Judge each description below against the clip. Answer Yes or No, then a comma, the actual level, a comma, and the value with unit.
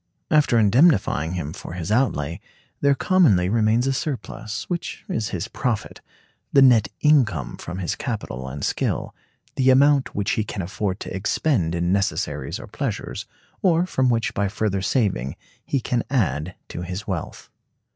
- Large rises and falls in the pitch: Yes, wide, 6.6 semitones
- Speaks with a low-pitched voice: Yes, low, 105 Hz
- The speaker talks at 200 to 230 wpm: No, average, 155 wpm